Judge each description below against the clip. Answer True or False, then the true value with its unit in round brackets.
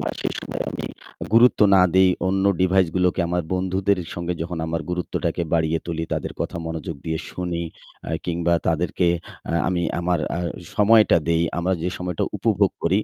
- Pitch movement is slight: True (2.0 semitones)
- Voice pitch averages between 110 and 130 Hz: False (90 Hz)